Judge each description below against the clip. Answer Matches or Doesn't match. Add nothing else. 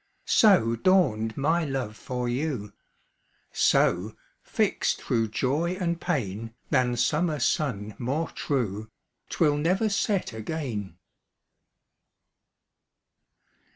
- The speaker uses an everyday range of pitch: Doesn't match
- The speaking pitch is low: Matches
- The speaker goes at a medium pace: Doesn't match